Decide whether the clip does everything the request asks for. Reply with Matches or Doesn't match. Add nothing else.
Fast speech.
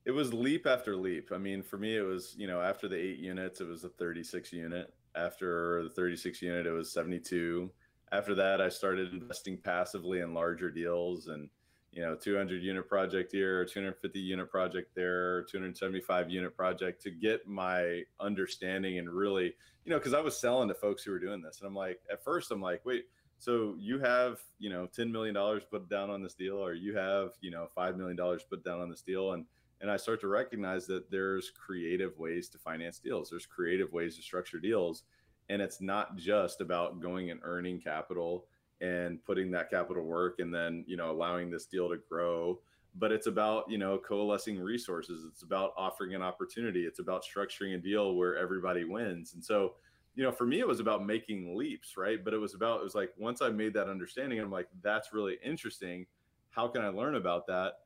Matches